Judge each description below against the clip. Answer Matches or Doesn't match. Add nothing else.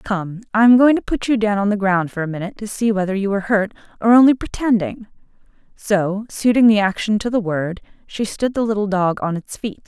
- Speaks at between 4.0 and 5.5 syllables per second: Doesn't match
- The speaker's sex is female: Matches